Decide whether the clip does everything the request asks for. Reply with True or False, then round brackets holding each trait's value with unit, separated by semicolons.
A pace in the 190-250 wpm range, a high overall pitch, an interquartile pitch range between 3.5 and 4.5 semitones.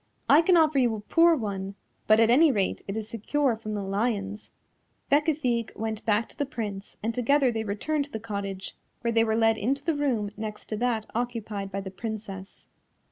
True (200 wpm; 225 Hz; 4.1 semitones)